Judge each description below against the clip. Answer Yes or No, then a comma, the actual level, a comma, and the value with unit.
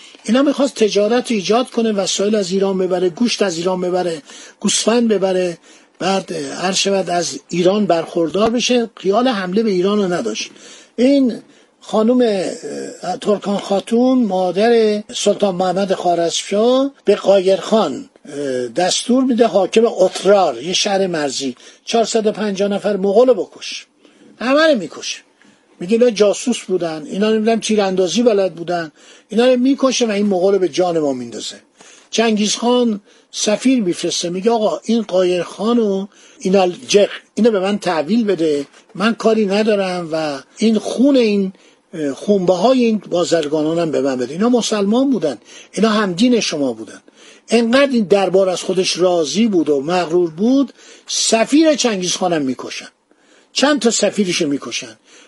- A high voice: Yes, high, 205 Hz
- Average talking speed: Yes, average, 135 wpm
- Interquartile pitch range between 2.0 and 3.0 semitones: No, average, 4.2 semitones